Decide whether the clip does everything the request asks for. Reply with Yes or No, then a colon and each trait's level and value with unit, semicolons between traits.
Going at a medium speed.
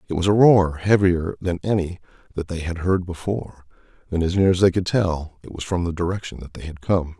No: fast, 235 wpm